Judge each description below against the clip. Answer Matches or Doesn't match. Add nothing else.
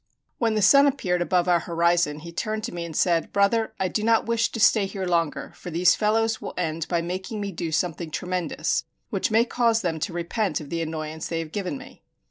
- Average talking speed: Doesn't match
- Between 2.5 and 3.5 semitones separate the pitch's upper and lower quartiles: Doesn't match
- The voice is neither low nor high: Matches